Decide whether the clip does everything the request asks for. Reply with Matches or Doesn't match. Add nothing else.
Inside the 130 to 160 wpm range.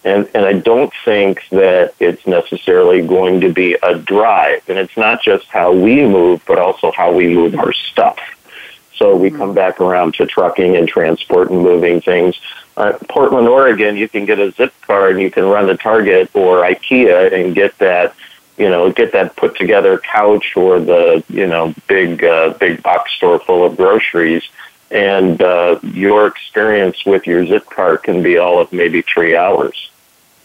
Doesn't match